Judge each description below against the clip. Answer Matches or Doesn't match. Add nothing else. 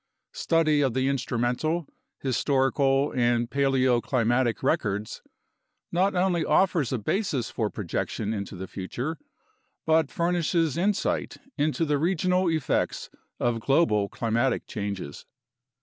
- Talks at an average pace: Doesn't match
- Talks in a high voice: Doesn't match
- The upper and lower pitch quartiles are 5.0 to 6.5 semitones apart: Matches